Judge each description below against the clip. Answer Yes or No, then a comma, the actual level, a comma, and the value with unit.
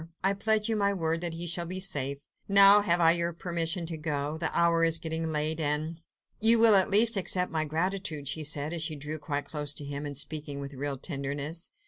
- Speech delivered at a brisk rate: Yes, fast, 225 wpm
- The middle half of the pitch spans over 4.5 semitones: No, average, 3.5 semitones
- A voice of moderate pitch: Yes, medium, 165 Hz